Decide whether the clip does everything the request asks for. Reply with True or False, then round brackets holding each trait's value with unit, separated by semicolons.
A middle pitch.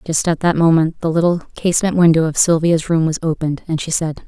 True (165 Hz)